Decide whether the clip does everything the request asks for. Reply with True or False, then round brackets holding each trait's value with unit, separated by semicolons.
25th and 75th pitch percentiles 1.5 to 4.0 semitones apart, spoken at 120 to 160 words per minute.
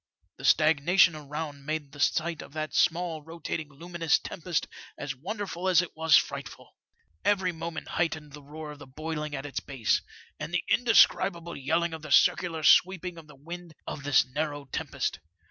False (2.7 semitones; 170 wpm)